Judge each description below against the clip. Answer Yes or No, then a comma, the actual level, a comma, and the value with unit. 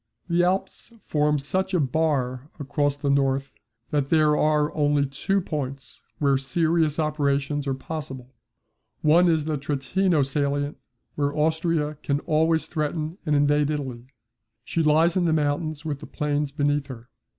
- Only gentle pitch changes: Yes, narrow, 2.2 semitones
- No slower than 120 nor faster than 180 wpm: Yes, average, 150 wpm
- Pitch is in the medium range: Yes, medium, 150 Hz